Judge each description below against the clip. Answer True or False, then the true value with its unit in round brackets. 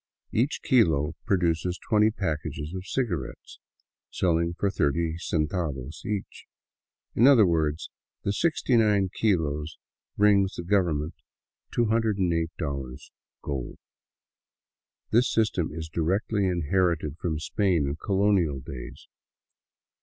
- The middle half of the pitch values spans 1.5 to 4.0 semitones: False (4.9 semitones)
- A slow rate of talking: True (100 wpm)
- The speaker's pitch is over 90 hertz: False (85 Hz)